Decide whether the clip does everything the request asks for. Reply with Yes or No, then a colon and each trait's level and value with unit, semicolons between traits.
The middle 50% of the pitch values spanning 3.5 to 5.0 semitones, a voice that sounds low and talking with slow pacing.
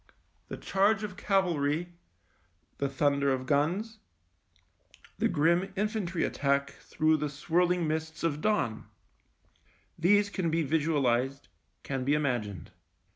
No: average, 4.5 semitones; medium, 155 Hz; slow, 115 wpm